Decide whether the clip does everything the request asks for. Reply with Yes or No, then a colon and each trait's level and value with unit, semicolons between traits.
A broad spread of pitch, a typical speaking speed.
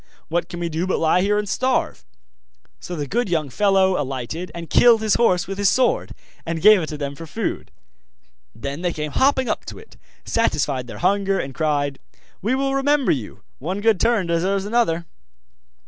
Yes: wide, 5.8 semitones; average, 190 wpm